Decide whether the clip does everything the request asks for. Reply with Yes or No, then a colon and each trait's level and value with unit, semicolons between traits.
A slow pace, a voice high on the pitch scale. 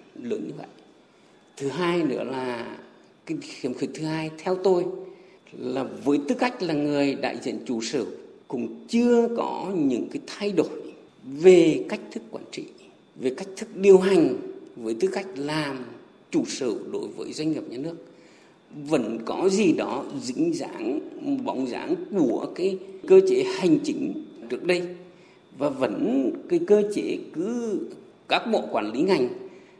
Yes: slow, 160 wpm; high, 240 Hz